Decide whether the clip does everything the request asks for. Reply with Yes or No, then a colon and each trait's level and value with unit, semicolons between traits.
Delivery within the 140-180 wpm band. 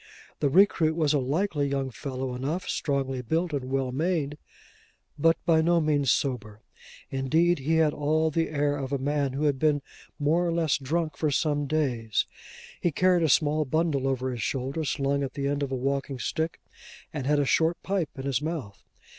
No: average, 190 wpm